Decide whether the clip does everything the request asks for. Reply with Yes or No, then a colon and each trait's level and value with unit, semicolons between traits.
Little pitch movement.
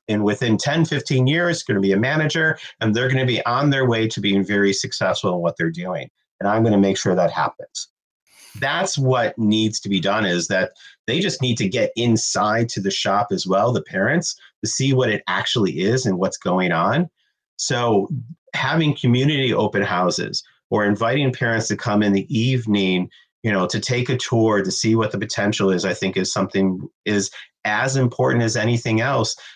No: average, 4.5 semitones